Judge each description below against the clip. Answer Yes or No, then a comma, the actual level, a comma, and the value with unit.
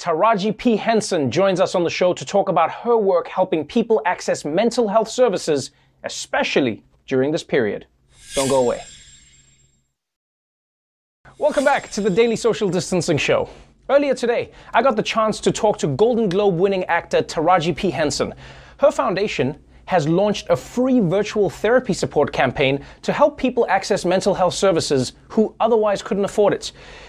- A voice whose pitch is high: Yes, high, 200 Hz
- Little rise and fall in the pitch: No, average, 4.3 semitones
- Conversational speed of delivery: Yes, average, 160 wpm